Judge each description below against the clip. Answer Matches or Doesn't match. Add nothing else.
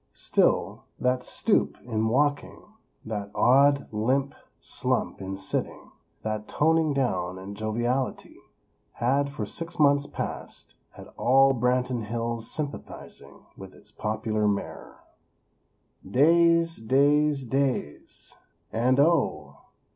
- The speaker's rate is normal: Doesn't match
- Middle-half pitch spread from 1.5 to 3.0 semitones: Doesn't match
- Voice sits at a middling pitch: Doesn't match